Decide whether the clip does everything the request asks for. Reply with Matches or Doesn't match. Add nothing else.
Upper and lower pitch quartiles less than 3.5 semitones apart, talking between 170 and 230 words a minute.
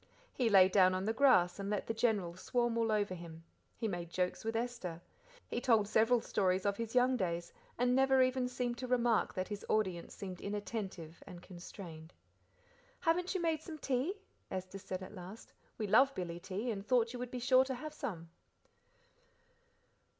Doesn't match